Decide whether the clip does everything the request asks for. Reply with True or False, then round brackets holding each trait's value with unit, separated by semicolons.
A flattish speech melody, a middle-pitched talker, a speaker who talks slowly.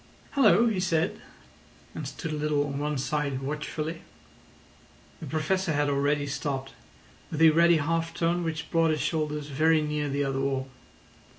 False (2.2 semitones; 150 Hz; 160 wpm)